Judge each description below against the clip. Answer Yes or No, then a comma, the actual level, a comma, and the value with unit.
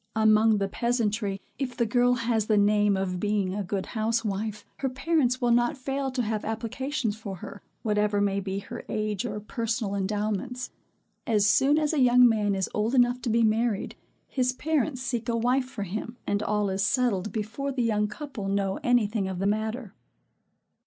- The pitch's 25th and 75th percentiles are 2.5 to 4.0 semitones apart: Yes, average, 3.1 semitones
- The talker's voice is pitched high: Yes, high, 220 Hz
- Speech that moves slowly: No, average, 185 wpm